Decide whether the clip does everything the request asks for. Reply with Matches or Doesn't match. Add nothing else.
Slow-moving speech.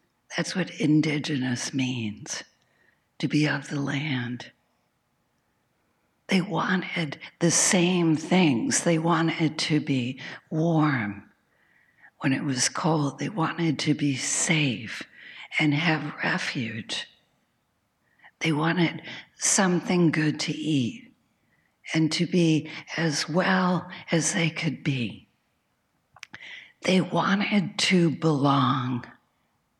Matches